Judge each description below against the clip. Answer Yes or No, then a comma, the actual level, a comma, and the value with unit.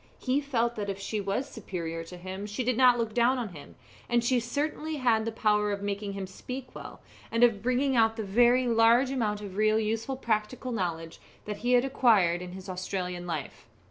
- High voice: Yes, high, 220 Hz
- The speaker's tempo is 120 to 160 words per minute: No, fast, 205 wpm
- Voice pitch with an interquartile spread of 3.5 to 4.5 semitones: Yes, average, 3.9 semitones